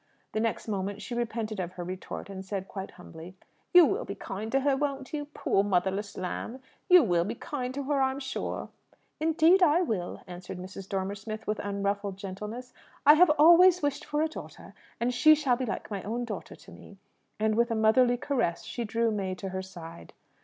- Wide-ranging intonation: Yes, wide, 6.0 semitones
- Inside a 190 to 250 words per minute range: Yes, fast, 205 wpm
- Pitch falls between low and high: No, high, 220 Hz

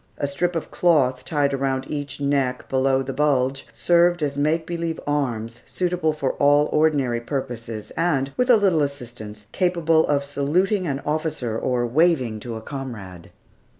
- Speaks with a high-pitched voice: No, medium, 140 Hz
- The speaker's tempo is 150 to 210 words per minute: Yes, average, 155 wpm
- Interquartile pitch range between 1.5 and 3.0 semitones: No, average, 4.0 semitones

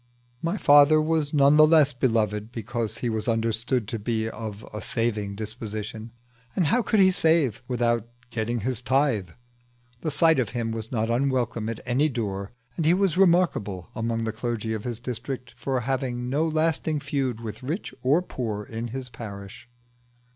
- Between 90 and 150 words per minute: No, average, 170 wpm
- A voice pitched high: No, low, 120 Hz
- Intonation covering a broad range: No, average, 4.4 semitones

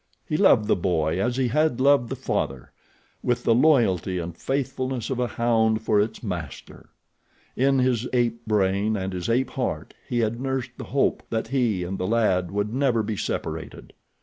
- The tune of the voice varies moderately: Yes, average, 4.7 semitones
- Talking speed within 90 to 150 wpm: No, average, 180 wpm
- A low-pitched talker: Yes, low, 115 Hz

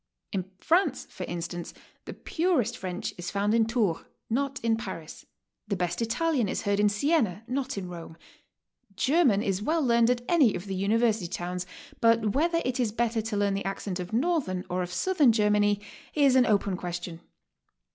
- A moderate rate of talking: Yes, average, 175 wpm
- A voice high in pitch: Yes, high, 210 Hz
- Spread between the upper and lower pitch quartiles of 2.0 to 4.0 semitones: No, average, 5.2 semitones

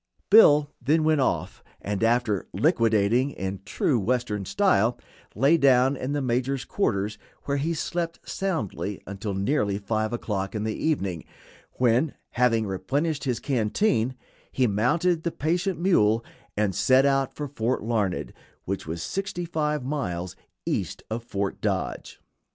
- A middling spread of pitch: No, wide, 6.2 semitones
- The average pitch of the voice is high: No, low, 125 Hz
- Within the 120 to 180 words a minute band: Yes, average, 140 wpm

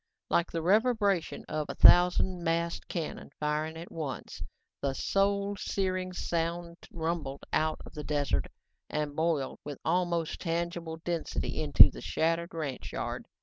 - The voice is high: No, medium, 165 Hz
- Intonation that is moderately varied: No, narrow, 2.3 semitones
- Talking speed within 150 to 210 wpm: No, average, 140 wpm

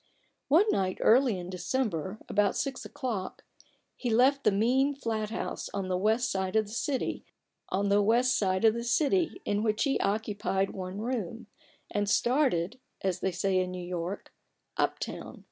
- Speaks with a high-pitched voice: Yes, high, 215 Hz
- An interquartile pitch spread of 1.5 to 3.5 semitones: No, average, 4.7 semitones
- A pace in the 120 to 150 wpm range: Yes, average, 145 wpm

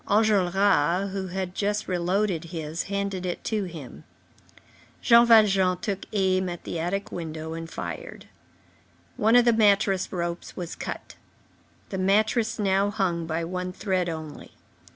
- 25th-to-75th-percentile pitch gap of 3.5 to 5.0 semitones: No, average, 2.8 semitones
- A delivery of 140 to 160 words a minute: Yes, average, 145 wpm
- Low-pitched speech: No, high, 190 Hz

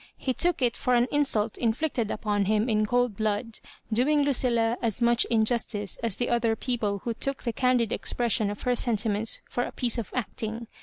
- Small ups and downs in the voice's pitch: Yes, narrow, 2.3 semitones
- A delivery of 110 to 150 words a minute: No, average, 195 wpm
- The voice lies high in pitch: Yes, high, 235 Hz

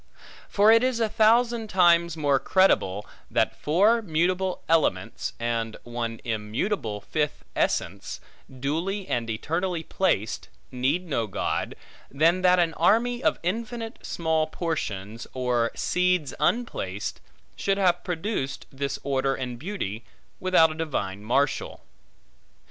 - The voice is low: No, medium, 160 Hz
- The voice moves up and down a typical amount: No, wide, 7.4 semitones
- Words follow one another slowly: Yes, slow, 120 wpm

